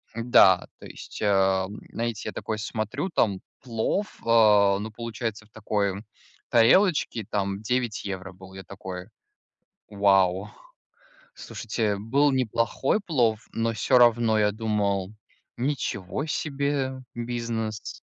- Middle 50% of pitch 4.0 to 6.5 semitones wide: No, average, 3.3 semitones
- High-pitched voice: No, low, 110 Hz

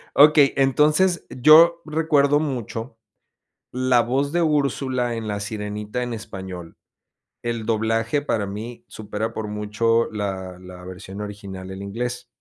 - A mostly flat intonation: No, average, 5.0 semitones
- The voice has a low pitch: Yes, low, 115 Hz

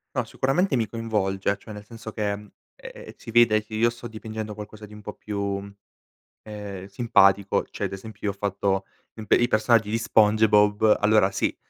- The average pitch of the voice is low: Yes, low, 105 Hz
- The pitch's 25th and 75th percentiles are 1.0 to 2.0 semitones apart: Yes, narrow, 1.6 semitones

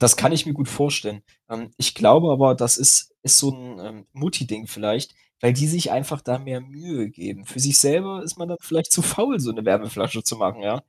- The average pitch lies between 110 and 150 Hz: Yes, low, 135 Hz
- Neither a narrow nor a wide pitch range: Yes, average, 4.8 semitones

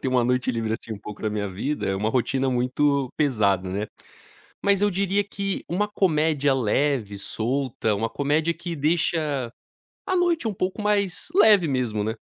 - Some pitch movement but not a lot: No, wide, 7.9 semitones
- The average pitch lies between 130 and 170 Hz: Yes, medium, 140 Hz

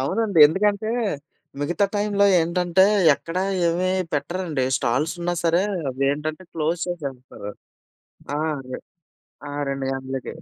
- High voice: No, medium, 165 Hz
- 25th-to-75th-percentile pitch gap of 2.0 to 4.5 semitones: No, average, 5.2 semitones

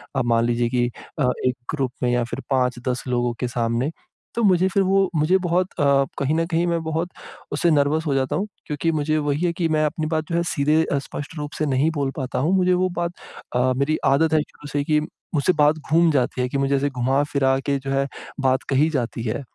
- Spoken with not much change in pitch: No, average, 3.6 semitones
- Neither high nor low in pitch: Yes, medium, 145 Hz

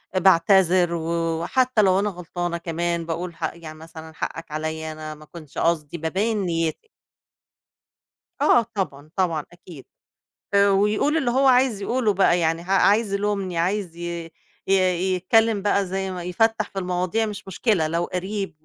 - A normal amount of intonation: Yes, average, 3.4 semitones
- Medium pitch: Yes, medium, 180 Hz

